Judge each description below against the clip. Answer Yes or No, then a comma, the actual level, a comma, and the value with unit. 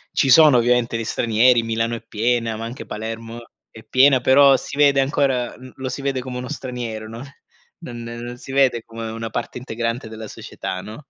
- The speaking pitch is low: Yes, low, 120 Hz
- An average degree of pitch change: No, narrow, 2.3 semitones